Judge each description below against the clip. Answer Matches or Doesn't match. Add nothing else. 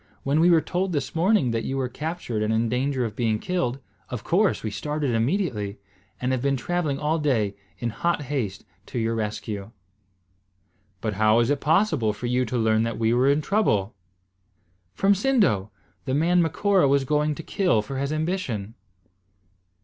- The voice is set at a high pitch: Doesn't match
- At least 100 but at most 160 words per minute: Doesn't match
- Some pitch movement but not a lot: Doesn't match